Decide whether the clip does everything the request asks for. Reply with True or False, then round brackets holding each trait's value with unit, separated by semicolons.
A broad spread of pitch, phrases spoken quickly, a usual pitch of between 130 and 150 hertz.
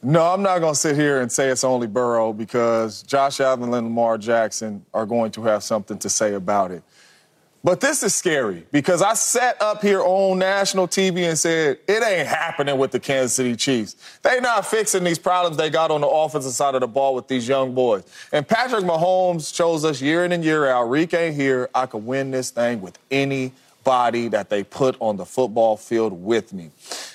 True (5.9 semitones; 210 wpm; 135 Hz)